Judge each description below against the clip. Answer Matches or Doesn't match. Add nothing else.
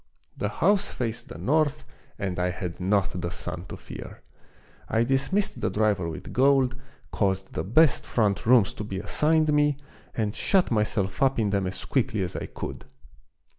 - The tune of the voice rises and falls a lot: Matches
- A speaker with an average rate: Matches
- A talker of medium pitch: Doesn't match